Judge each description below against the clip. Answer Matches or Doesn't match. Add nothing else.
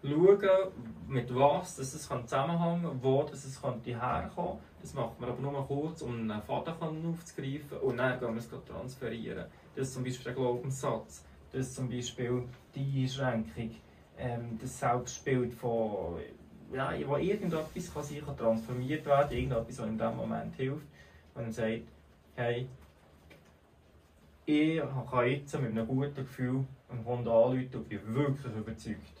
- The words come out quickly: Doesn't match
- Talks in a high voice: Doesn't match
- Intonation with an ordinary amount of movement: Matches